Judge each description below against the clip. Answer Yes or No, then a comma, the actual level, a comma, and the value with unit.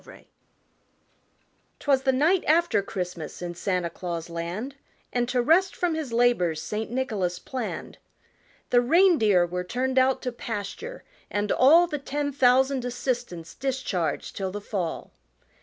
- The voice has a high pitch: Yes, high, 245 Hz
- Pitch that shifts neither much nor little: No, wide, 6.9 semitones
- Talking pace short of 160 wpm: Yes, average, 140 wpm